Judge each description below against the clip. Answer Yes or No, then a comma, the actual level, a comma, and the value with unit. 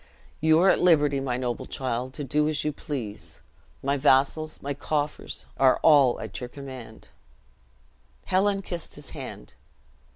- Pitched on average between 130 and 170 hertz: Yes, medium, 140 Hz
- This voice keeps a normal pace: Yes, average, 150 wpm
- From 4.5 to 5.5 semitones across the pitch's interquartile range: No, average, 3.2 semitones